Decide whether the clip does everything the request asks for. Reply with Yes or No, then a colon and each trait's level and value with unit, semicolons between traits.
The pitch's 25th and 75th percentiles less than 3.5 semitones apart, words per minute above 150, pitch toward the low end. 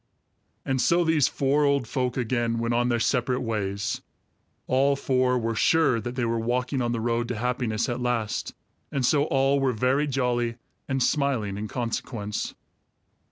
Yes: narrow, 2.6 semitones; average, 165 wpm; low, 125 Hz